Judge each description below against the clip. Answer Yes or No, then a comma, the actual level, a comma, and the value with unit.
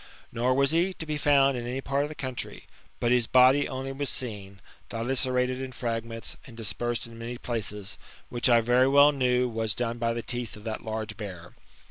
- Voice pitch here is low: Yes, low, 120 Hz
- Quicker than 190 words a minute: Yes, average, 200 wpm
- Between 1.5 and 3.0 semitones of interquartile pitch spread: Yes, narrow, 2.5 semitones